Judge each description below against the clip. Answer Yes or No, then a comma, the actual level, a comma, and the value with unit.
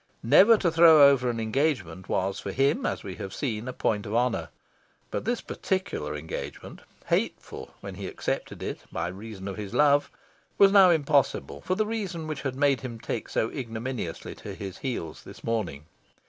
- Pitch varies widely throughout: Yes, wide, 7.5 semitones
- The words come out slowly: No, average, 180 wpm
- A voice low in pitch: Yes, low, 125 Hz